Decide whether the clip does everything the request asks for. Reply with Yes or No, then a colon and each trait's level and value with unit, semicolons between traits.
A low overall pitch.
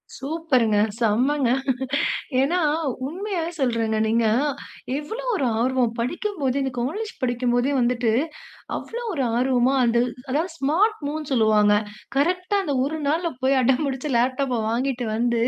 No: very high, 265 Hz